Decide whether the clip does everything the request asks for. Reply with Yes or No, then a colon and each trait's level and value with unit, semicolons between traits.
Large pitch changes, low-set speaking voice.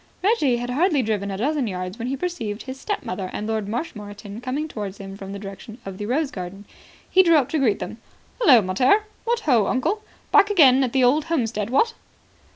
No: wide, 6.8 semitones; high, 245 Hz